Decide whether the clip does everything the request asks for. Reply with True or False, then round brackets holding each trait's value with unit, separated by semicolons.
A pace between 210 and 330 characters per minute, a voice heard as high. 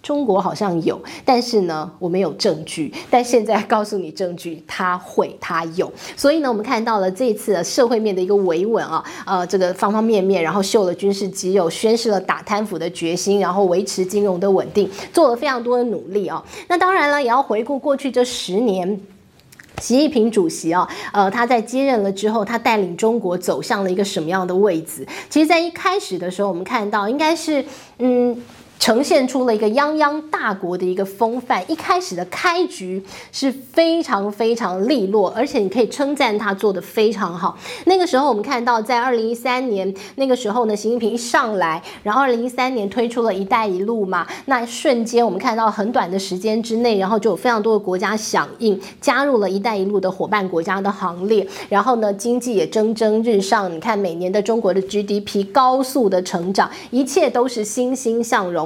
True (310 characters per minute; 220 Hz)